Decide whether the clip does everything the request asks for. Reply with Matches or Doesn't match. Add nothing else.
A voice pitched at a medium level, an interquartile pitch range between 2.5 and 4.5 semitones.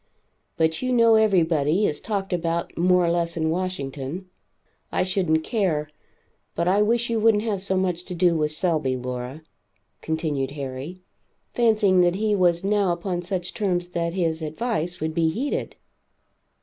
Matches